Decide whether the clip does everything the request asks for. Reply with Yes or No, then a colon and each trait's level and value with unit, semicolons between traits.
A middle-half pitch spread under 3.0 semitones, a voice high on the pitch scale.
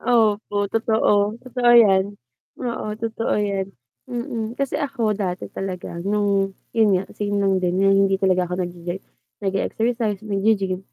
Yes: narrow, 2.6 semitones; high, 205 Hz